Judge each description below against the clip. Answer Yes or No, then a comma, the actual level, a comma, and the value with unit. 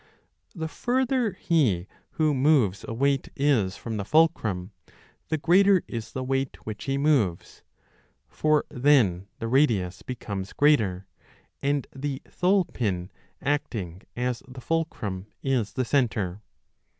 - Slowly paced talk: Yes, slow, 125 wpm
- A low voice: Yes, low, 130 Hz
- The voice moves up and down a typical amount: No, wide, 6.5 semitones